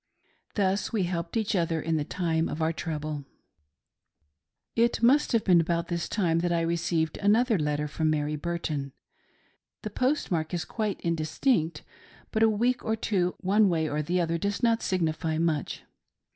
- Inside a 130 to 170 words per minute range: Yes, average, 165 wpm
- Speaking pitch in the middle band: Yes, medium, 170 Hz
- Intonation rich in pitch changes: No, average, 4.4 semitones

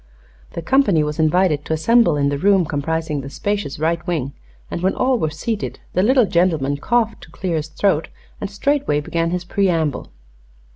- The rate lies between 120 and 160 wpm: No, average, 180 wpm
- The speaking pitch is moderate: Yes, medium, 170 Hz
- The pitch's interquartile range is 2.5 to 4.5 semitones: No, average, 4.9 semitones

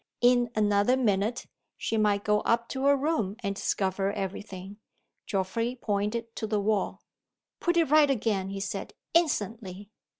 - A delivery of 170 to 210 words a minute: No, average, 155 wpm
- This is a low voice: No, high, 210 Hz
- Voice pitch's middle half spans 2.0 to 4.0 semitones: Yes, average, 3.4 semitones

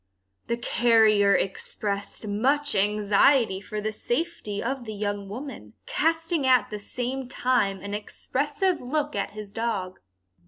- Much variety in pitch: No, average, 4.7 semitones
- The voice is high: Yes, high, 225 Hz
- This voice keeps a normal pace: No, slow, 130 wpm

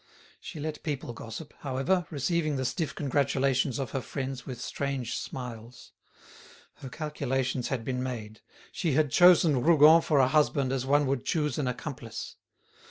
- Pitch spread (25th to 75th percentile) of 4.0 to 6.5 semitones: No, average, 3.0 semitones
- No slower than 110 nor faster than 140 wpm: No, average, 155 wpm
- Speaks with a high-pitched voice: No, low, 135 Hz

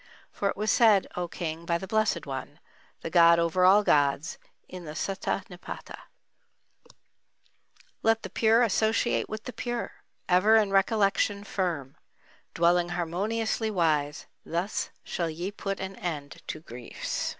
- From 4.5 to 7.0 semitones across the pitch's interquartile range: No, average, 4.0 semitones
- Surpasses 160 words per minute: No, average, 140 wpm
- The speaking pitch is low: No, medium, 185 Hz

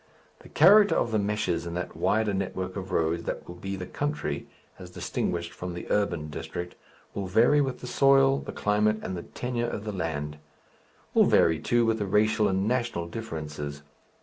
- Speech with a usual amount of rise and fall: Yes, average, 4.9 semitones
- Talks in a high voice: No, low, 100 Hz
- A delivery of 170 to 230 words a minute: Yes, average, 185 wpm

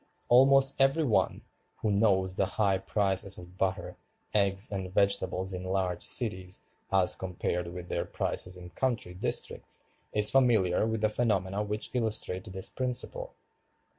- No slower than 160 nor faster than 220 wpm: No, average, 140 wpm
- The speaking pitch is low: Yes, low, 100 Hz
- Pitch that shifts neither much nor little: Yes, average, 3.3 semitones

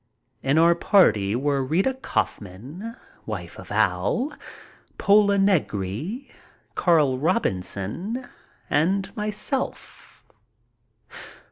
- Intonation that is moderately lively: No, wide, 8.3 semitones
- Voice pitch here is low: No, medium, 170 Hz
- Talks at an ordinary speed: No, slow, 80 wpm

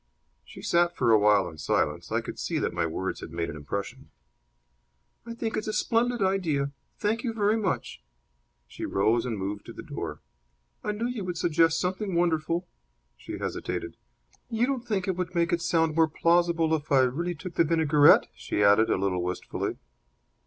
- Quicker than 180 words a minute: Yes, average, 190 wpm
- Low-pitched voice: No, medium, 165 Hz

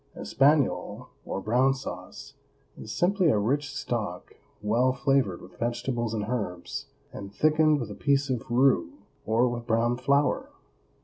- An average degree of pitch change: Yes, average, 4.2 semitones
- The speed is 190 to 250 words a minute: No, average, 140 wpm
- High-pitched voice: No, low, 120 Hz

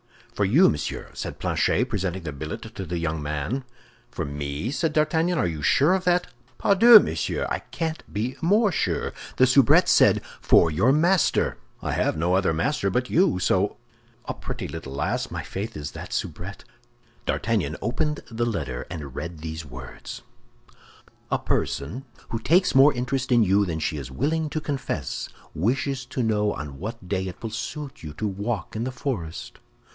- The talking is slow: No, average, 175 wpm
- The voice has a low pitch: Yes, low, 105 Hz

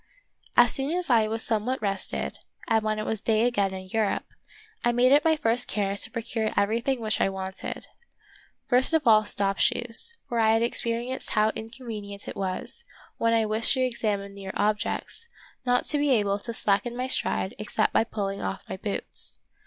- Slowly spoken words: No, average, 190 wpm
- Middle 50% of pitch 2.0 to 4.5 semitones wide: Yes, average, 3.2 semitones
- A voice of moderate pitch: No, high, 225 Hz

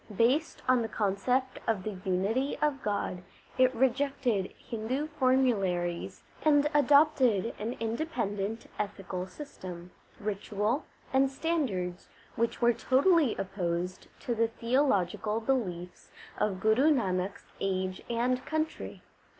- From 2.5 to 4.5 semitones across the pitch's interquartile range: No, wide, 5.4 semitones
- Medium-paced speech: No, slow, 115 wpm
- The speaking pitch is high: Yes, high, 230 Hz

